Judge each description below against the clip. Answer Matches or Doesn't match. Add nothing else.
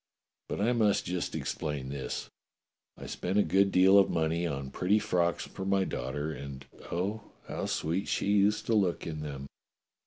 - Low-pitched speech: Matches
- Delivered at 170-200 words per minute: Matches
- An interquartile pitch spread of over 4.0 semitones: Matches